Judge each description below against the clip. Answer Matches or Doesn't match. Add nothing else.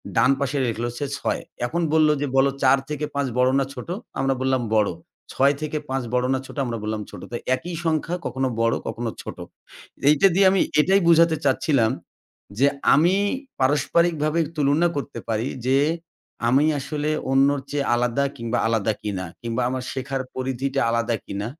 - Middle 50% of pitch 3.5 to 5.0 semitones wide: Matches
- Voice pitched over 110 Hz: Matches